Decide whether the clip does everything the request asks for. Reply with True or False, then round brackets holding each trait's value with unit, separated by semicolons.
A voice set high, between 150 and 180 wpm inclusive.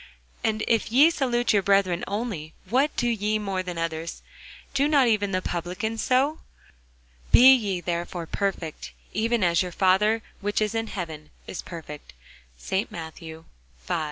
True (200 Hz; 155 wpm)